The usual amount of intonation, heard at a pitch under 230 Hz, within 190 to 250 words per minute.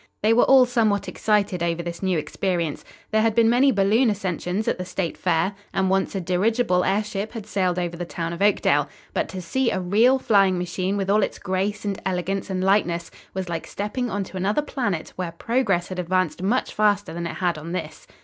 Yes: average, 3.0 semitones; high, 190 Hz; fast, 205 wpm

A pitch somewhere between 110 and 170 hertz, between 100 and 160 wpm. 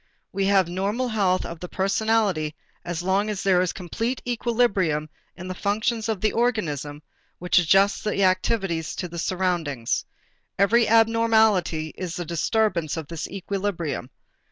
No: high, 190 Hz; average, 150 wpm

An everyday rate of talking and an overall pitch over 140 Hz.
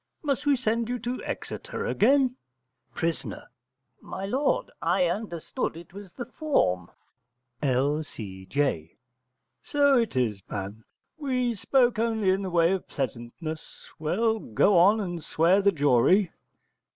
No: slow, 125 wpm; medium, 185 Hz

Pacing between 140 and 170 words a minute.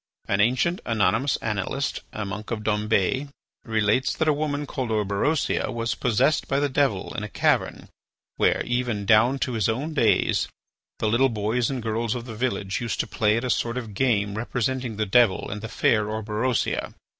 No: average, 180 wpm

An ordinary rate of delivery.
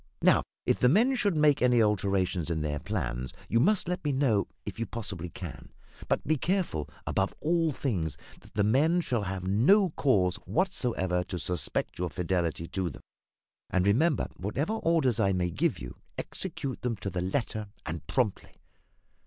Yes: average, 170 wpm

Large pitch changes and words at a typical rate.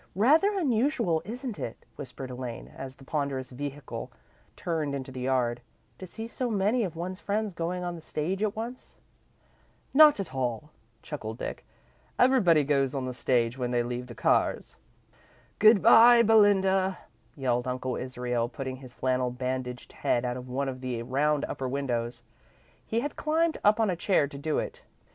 Yes: wide, 8.2 semitones; average, 170 wpm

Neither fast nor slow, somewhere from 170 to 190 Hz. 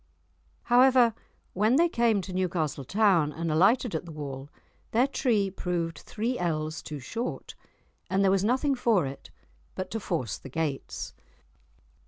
Yes: average, 150 wpm; medium, 185 Hz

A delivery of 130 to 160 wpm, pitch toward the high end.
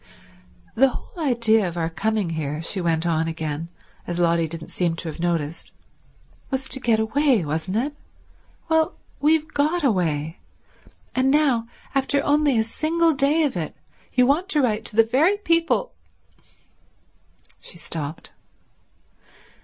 Yes: average, 145 wpm; high, 225 Hz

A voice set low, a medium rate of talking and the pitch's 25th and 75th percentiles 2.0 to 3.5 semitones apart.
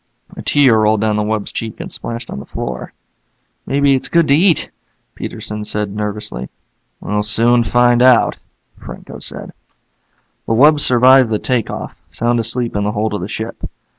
Yes: low, 115 Hz; average, 170 wpm; average, 3.1 semitones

